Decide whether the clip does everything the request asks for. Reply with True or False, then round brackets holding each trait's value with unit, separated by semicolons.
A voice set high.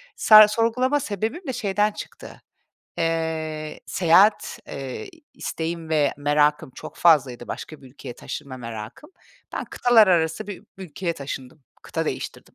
False (165 Hz)